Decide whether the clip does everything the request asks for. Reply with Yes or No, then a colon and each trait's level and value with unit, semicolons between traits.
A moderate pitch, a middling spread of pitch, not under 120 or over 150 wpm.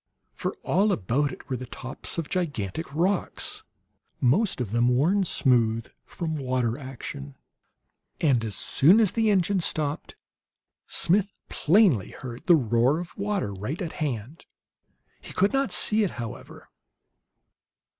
No: medium, 145 Hz; wide, 7.4 semitones; slow, 135 wpm